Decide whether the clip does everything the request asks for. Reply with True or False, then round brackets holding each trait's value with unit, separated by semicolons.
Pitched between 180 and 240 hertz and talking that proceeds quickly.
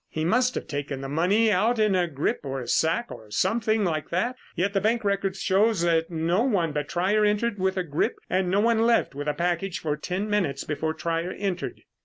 True (185 Hz; 220 wpm)